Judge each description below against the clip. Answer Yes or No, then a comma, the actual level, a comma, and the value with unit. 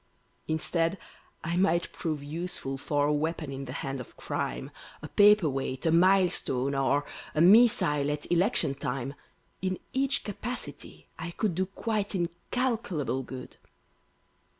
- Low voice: No, medium, 165 Hz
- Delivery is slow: Yes, slow, 130 wpm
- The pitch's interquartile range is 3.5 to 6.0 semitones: Yes, wide, 5.4 semitones